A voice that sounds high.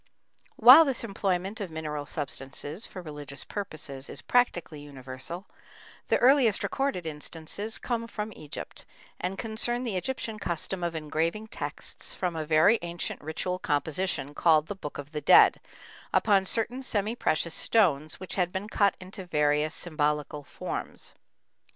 No: medium, 175 Hz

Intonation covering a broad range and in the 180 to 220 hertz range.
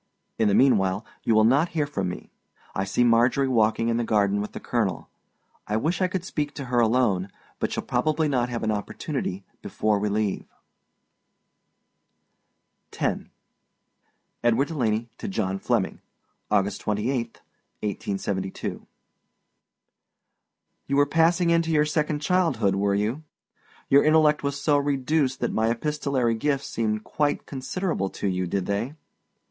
No: wide, 5.9 semitones; low, 120 Hz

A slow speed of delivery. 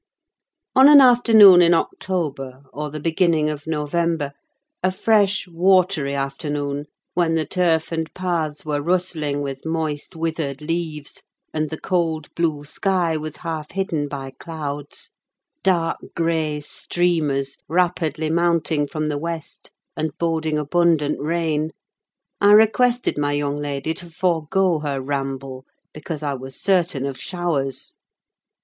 Yes: slow, 125 wpm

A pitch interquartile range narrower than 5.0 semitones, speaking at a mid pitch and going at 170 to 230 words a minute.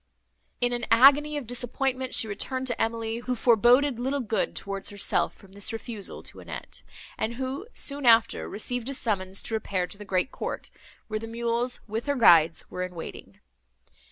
No: average, 3.6 semitones; high, 230 Hz; average, 180 wpm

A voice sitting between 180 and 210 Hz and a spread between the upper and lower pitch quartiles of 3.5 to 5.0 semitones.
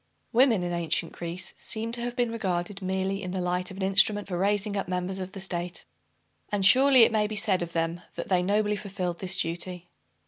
No: high, 190 Hz; average, 2.7 semitones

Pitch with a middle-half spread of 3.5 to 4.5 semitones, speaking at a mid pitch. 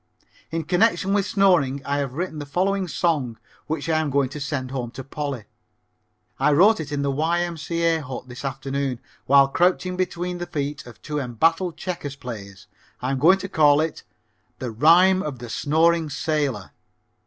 Yes: average, 4.1 semitones; medium, 150 Hz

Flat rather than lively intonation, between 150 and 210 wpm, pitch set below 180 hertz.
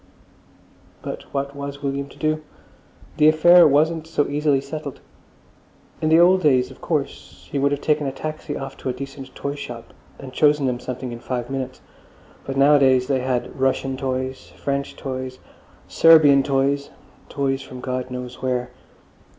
Yes: narrow, 2.0 semitones; average, 155 wpm; medium, 140 Hz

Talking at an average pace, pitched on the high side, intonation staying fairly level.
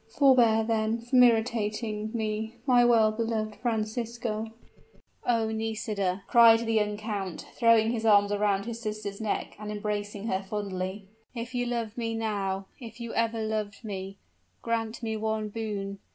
Yes: average, 150 wpm; high, 220 Hz; narrow, 1.8 semitones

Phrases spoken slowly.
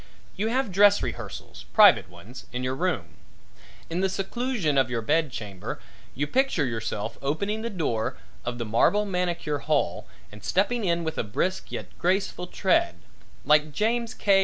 No: average, 160 wpm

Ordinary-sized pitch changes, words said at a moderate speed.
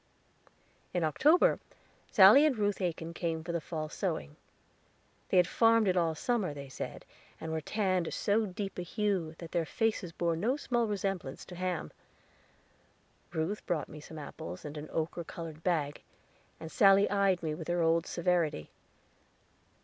Yes: average, 3.7 semitones; average, 160 wpm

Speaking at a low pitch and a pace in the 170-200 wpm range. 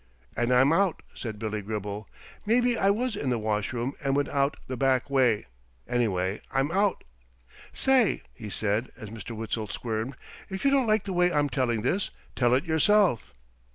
Yes: low, 130 Hz; average, 175 wpm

